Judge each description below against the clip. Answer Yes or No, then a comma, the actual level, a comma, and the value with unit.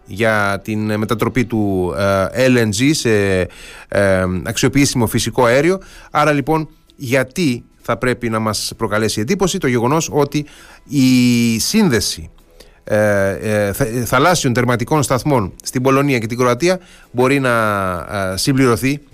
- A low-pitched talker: Yes, low, 120 Hz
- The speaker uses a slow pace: Yes, slow, 105 wpm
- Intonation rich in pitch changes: No, average, 4.6 semitones